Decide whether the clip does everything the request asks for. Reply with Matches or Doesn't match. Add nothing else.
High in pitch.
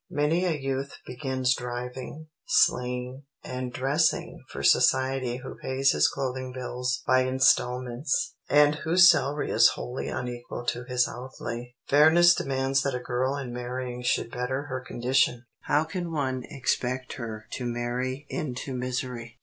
Doesn't match